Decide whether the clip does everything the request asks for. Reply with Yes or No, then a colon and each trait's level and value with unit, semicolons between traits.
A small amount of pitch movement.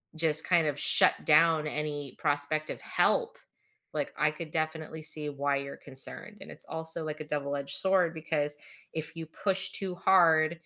Yes: narrow, 1.9 semitones